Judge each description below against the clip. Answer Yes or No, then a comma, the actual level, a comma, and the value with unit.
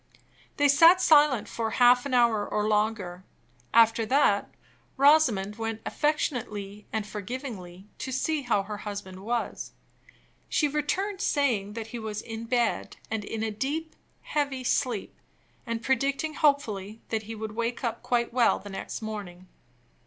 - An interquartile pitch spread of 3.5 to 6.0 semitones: Yes, average, 4.7 semitones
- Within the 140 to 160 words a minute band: Yes, average, 145 wpm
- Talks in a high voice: Yes, high, 230 Hz